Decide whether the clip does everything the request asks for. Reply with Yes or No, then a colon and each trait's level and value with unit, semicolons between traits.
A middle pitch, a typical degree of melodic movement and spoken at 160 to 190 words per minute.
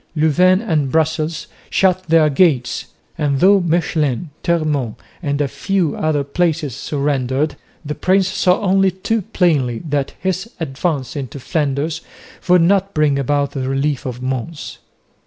No: medium, 155 Hz; average, 4.3 semitones; average, 140 wpm